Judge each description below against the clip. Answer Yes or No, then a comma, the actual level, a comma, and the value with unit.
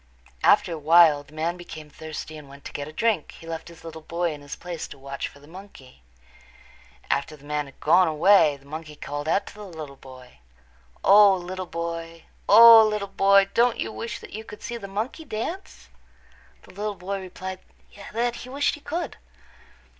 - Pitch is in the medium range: Yes, medium, 170 Hz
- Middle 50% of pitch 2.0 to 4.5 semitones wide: No, average, 5.2 semitones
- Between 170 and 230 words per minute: Yes, average, 195 wpm